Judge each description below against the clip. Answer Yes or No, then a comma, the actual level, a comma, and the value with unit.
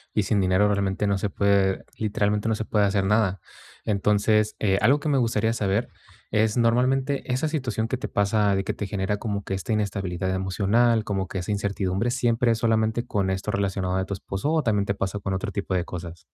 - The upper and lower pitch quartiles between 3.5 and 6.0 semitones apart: No, narrow, 2.6 semitones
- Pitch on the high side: No, low, 105 Hz